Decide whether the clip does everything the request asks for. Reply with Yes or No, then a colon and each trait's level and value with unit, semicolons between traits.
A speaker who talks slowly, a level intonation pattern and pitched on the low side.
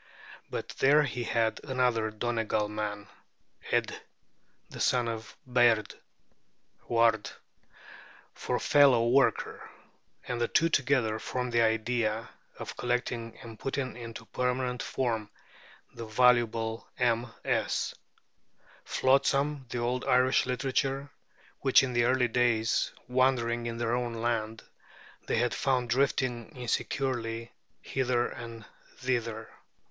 Yes: slow, 110 wpm; narrow, 2.0 semitones; low, 120 Hz